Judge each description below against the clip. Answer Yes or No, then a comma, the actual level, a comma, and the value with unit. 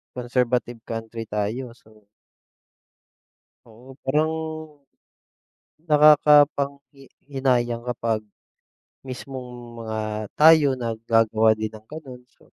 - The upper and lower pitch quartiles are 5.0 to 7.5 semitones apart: No, average, 3.7 semitones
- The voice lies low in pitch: Yes, low, 125 Hz